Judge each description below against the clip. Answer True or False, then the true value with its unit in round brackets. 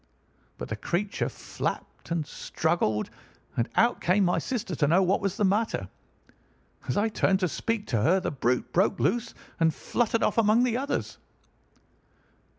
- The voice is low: False (190 Hz)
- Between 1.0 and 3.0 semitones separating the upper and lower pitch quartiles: False (5.3 semitones)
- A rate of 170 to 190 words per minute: False (160 wpm)